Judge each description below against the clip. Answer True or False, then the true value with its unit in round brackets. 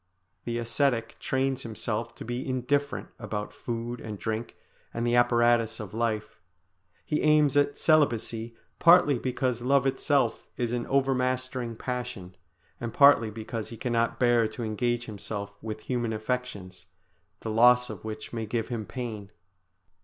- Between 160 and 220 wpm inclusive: False (145 wpm)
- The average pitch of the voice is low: True (120 Hz)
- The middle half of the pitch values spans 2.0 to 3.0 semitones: True (2.4 semitones)